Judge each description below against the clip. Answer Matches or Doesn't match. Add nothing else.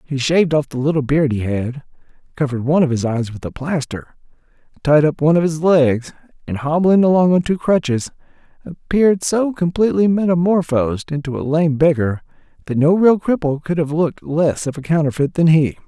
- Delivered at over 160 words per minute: Matches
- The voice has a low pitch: Doesn't match